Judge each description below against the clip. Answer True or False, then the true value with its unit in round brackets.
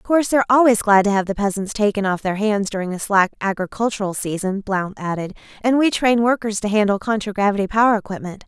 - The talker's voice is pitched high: True (210 Hz)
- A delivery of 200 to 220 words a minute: True (205 wpm)